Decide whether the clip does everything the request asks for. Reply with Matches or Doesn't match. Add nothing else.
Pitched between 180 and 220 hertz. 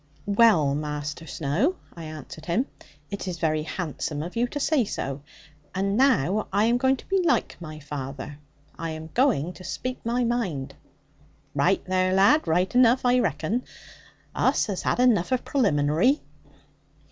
Matches